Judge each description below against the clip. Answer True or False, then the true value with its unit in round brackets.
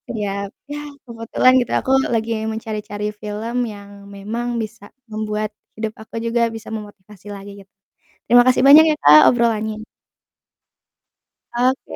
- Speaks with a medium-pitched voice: False (220 Hz)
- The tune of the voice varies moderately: False (2.1 semitones)